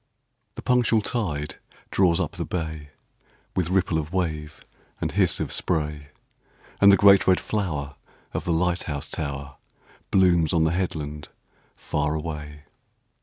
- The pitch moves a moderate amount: Yes, average, 3.7 semitones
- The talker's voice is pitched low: Yes, very low, 80 Hz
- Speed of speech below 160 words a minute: Yes, average, 140 wpm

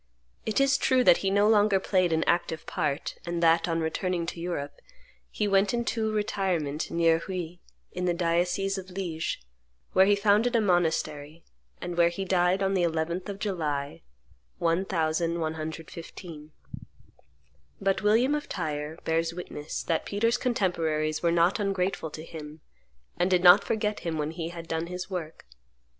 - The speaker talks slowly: No, average, 155 wpm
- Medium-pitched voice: Yes, medium, 175 Hz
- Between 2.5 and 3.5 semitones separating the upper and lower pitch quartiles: Yes, average, 3.2 semitones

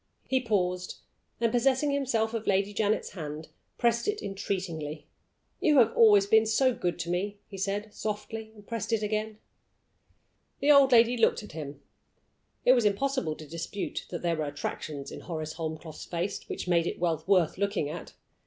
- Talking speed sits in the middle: Yes, average, 170 wpm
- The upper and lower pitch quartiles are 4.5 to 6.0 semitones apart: Yes, average, 5.2 semitones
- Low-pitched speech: No, high, 200 Hz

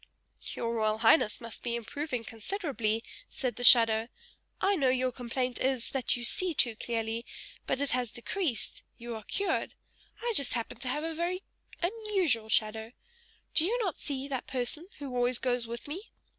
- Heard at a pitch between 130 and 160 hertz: No, very high, 250 Hz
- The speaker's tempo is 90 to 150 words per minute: No, average, 170 wpm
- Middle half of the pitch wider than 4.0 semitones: Yes, average, 5.1 semitones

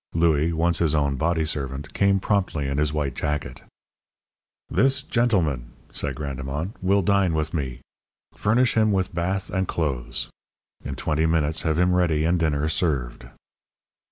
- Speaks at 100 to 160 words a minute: Yes, average, 150 wpm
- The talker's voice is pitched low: Yes, very low, 80 Hz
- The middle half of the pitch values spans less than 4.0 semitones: No, average, 4.3 semitones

